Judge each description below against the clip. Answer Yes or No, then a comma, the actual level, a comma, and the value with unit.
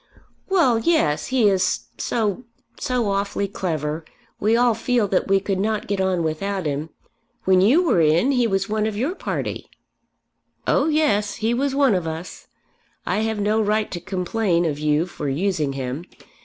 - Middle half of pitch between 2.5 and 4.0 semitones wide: No, average, 4.8 semitones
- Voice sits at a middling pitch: No, high, 200 Hz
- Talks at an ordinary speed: Yes, average, 170 wpm